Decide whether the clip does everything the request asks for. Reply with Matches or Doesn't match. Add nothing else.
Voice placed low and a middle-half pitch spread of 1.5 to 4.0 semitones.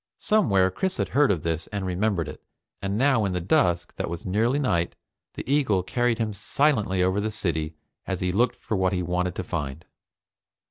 Doesn't match